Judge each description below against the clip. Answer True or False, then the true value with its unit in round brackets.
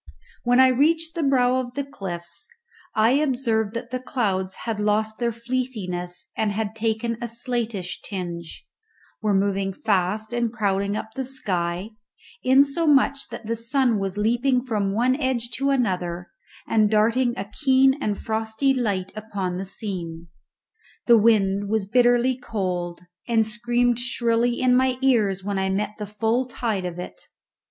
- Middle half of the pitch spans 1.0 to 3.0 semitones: False (4.0 semitones)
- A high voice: True (225 Hz)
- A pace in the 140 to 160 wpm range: True (150 wpm)